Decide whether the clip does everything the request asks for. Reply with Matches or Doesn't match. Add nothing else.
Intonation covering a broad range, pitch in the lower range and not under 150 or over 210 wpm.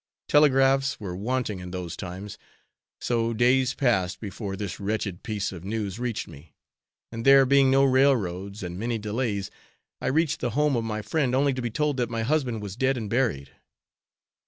Doesn't match